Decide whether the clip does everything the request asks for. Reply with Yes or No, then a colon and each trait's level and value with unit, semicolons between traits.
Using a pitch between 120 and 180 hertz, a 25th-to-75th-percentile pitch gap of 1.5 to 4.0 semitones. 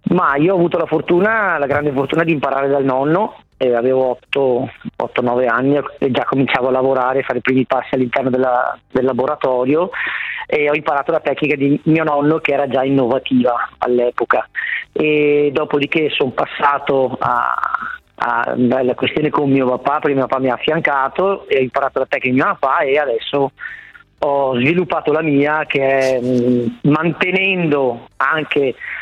Yes: medium, 140 Hz; average, 3.2 semitones